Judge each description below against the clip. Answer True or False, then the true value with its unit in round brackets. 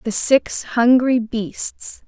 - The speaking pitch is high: True (240 Hz)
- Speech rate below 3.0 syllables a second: True (2.6 syllables/s)